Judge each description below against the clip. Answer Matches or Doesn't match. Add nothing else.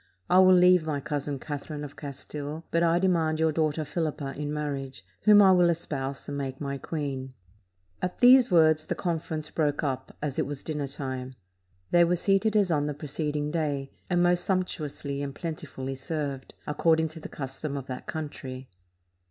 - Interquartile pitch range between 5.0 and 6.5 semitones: Doesn't match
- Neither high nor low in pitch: Matches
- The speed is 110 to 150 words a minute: Doesn't match